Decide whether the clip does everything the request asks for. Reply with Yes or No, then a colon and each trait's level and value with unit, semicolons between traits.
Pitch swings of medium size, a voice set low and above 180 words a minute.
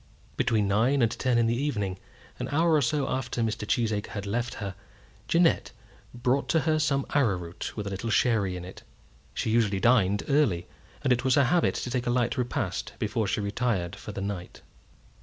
Yes: average, 4.5 semitones; low, 115 Hz; average, 195 wpm